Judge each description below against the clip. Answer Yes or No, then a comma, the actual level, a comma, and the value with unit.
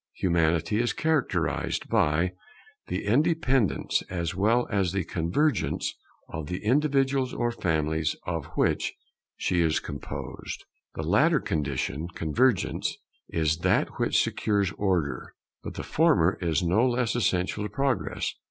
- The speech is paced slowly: Yes, slow, 130 wpm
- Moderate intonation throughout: No, wide, 7.0 semitones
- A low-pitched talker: Yes, very low, 95 Hz